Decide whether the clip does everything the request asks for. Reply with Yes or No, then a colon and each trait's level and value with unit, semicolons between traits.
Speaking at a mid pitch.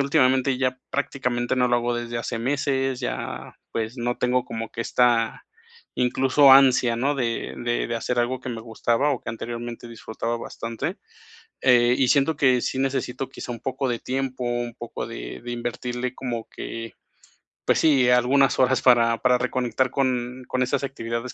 No: low, 125 Hz